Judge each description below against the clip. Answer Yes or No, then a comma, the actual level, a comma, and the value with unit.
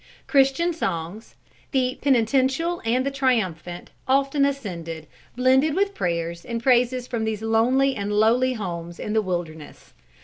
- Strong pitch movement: Yes, wide, 6.4 semitones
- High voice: Yes, high, 235 Hz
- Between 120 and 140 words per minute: Yes, slow, 135 wpm